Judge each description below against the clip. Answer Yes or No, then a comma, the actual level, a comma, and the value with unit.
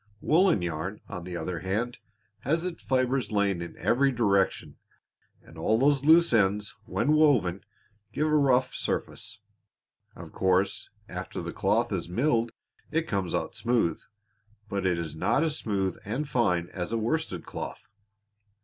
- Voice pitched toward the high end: No, low, 110 Hz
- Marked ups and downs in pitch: Yes, wide, 6.5 semitones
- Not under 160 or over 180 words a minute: No, average, 150 wpm